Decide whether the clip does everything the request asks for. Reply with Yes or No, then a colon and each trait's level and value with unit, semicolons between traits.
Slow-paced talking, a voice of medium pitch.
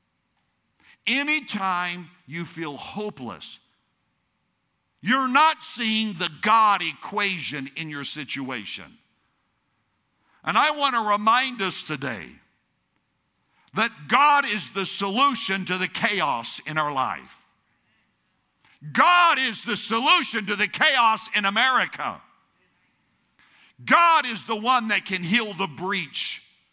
No: slow, 110 wpm; high, 210 Hz